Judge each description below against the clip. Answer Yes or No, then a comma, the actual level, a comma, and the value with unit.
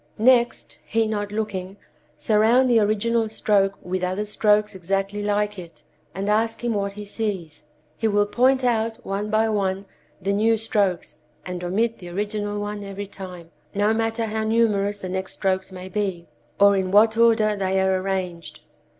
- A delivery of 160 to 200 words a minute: Yes, average, 165 wpm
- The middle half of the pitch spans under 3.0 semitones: Yes, narrow, 2.5 semitones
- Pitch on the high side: Yes, high, 205 Hz